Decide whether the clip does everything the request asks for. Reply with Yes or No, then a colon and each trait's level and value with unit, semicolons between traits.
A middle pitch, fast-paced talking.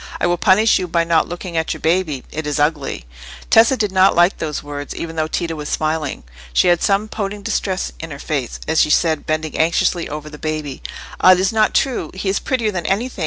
Yes: medium, 165 Hz; fast, 225 wpm